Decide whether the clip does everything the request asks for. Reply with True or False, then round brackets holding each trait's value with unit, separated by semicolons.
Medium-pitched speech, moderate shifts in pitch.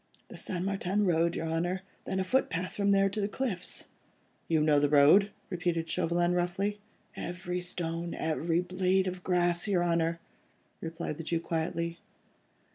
False (175 Hz; 2.2 semitones)